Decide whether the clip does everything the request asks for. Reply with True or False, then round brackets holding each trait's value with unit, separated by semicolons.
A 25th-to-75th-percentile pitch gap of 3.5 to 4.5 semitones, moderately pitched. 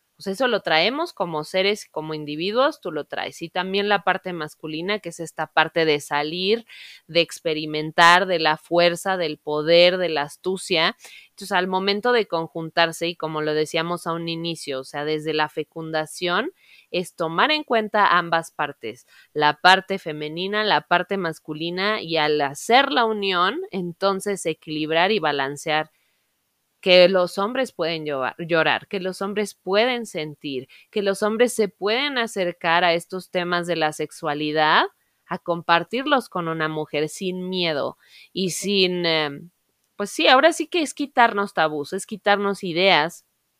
True (4.0 semitones; 175 Hz)